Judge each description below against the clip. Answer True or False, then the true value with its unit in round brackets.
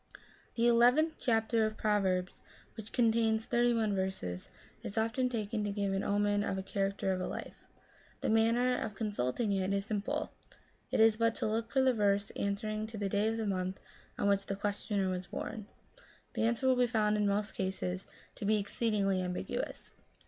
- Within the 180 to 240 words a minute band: True (185 wpm)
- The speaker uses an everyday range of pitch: False (2.3 semitones)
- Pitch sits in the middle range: False (210 Hz)